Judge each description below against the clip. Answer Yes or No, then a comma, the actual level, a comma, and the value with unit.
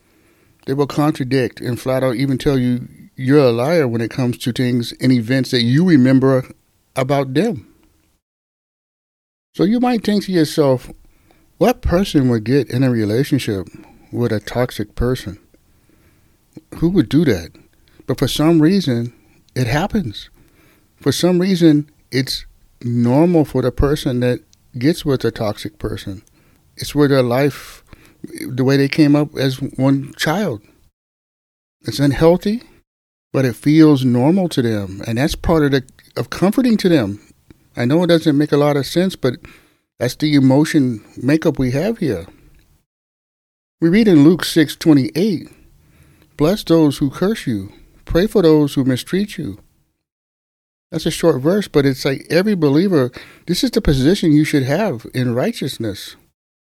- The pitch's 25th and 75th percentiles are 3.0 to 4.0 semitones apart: No, average, 4.6 semitones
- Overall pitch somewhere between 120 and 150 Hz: Yes, medium, 140 Hz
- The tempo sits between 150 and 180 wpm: Yes, average, 155 wpm